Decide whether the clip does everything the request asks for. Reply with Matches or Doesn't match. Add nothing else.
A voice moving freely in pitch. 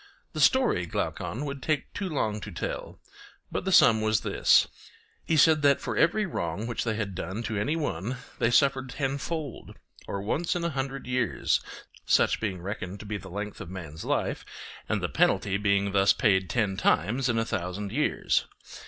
Matches